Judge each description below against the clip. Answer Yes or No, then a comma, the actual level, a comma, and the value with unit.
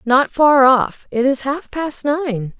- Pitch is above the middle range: Yes, very high, 270 Hz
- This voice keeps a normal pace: Yes, average, 160 wpm